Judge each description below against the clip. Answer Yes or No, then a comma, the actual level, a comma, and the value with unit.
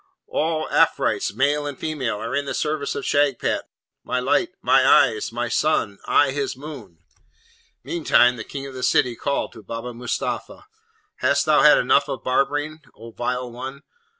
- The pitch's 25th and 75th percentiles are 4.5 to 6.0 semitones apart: No, average, 3.3 semitones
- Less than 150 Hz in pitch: Yes, low, 135 Hz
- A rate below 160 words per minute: No, average, 165 wpm